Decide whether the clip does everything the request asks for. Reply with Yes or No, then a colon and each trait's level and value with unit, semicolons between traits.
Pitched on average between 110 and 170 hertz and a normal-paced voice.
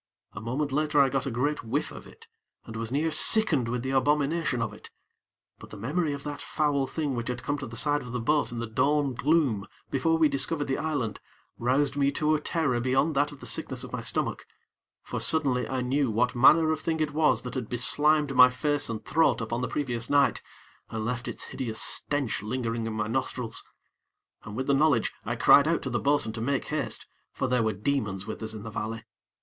No: low, 135 Hz; fast, 220 wpm